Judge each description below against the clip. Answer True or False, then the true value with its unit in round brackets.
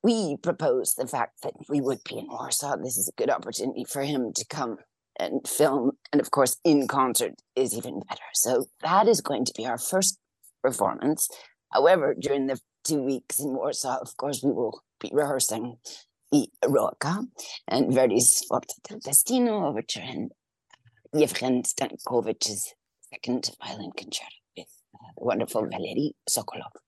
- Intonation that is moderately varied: False (6.7 semitones)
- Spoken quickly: False (155 wpm)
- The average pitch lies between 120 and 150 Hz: True (140 Hz)